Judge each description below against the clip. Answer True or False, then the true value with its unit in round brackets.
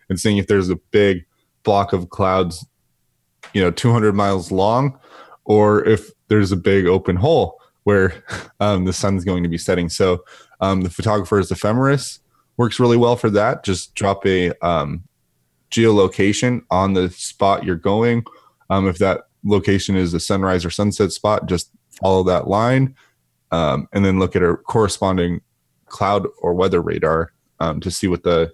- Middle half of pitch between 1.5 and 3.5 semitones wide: True (2.5 semitones)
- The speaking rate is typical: True (165 wpm)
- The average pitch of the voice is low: True (95 Hz)